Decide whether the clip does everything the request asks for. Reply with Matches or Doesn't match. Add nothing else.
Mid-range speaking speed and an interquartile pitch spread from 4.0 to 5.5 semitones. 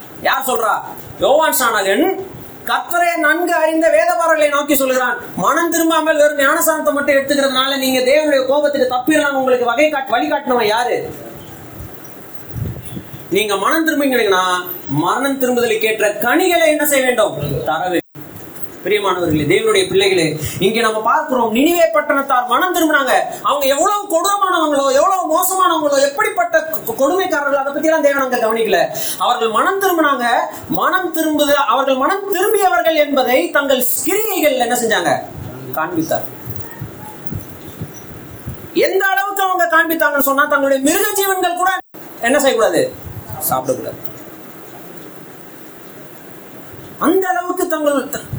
Matches